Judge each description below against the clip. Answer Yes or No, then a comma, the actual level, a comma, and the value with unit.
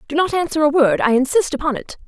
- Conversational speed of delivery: No, fast, 260 wpm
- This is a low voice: No, very high, 295 Hz